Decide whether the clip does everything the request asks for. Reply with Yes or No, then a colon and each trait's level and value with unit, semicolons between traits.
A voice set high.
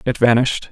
No: low, 120 Hz